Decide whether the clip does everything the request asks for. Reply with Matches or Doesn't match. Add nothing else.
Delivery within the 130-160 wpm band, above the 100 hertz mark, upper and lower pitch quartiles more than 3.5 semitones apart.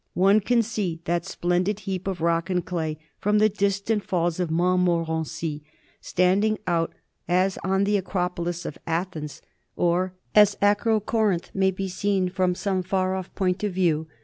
Doesn't match